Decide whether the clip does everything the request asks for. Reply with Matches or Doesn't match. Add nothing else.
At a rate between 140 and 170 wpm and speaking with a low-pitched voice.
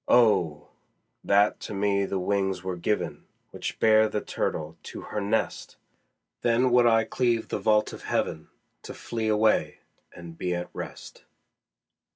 Matches